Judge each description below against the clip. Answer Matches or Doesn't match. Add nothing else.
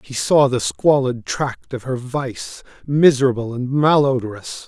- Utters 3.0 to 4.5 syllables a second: Matches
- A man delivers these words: Matches